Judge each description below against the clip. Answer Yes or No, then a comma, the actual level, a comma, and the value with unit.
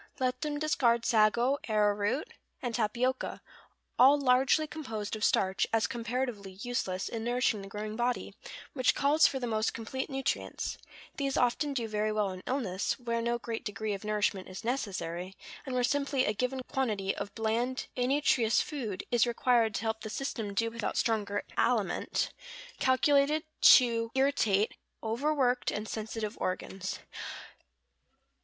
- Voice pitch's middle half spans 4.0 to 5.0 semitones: No, average, 3.5 semitones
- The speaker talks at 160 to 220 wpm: No, average, 145 wpm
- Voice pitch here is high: Yes, high, 230 Hz